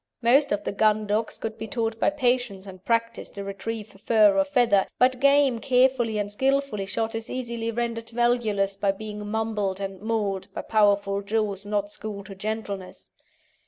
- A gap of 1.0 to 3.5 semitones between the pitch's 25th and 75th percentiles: Yes, average, 2.8 semitones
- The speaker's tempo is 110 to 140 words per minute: No, average, 170 wpm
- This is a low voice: No, high, 220 Hz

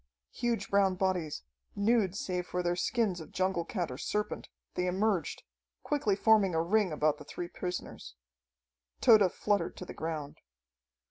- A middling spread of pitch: Yes, average, 3.3 semitones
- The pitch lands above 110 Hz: Yes, medium, 185 Hz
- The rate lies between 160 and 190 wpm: No, average, 150 wpm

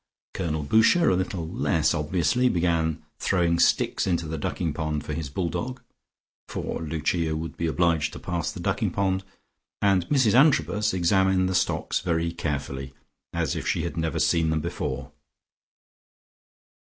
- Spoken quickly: No, average, 155 wpm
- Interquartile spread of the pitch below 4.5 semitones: Yes, average, 2.9 semitones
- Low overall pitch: Yes, very low, 85 Hz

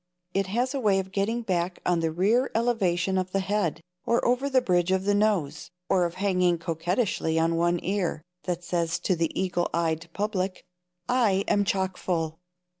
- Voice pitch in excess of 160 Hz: Yes, medium, 185 Hz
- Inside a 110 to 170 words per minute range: No, average, 180 wpm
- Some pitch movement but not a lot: Yes, average, 3.1 semitones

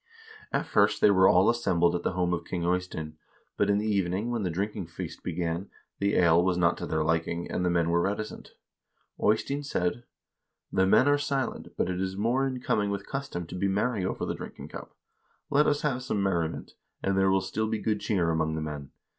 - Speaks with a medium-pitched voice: No, very low, 95 Hz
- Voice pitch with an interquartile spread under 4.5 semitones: Yes, average, 3.8 semitones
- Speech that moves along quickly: Yes, fast, 215 wpm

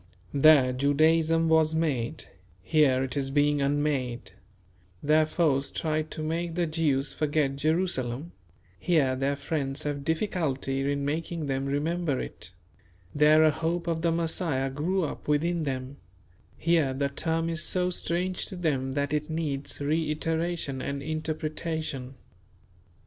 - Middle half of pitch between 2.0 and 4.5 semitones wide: Yes, average, 2.8 semitones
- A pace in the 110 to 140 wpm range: Yes, slow, 135 wpm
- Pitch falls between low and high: Yes, medium, 150 Hz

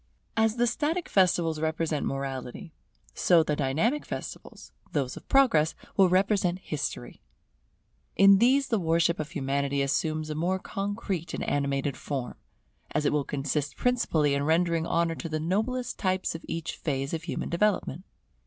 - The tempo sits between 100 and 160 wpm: Yes, average, 155 wpm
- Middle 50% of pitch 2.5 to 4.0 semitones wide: No, average, 5.0 semitones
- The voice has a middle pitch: Yes, medium, 165 Hz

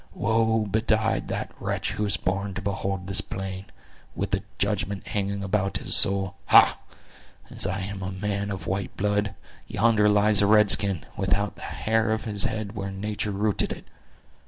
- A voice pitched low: Yes, low, 100 Hz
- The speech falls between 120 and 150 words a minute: No, average, 170 wpm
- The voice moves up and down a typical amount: No, narrow, 1.5 semitones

